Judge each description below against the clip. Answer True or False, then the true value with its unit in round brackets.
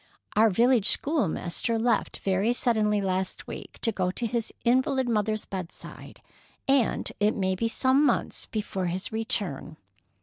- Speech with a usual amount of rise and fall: True (4.0 semitones)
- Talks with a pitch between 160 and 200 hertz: False (215 Hz)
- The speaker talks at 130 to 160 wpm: True (140 wpm)